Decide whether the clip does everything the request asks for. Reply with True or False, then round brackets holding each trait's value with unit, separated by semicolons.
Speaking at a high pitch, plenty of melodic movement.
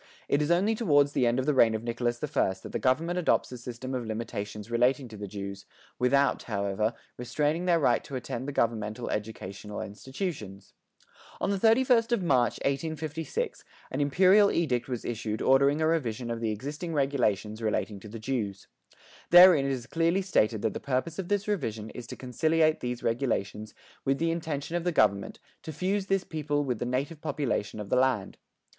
False (130 Hz; 6.2 semitones)